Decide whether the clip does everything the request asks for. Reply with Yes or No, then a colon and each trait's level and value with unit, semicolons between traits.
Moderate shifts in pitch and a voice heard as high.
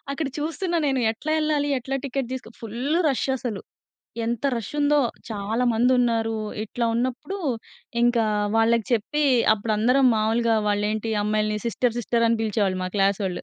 Yes: average, 3.2 semitones; high, 235 Hz